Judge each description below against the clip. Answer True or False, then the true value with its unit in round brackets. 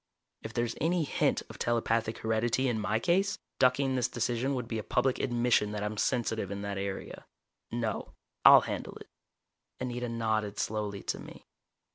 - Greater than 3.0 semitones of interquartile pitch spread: False (2.5 semitones)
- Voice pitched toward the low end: True (115 Hz)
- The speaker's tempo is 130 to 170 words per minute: True (165 wpm)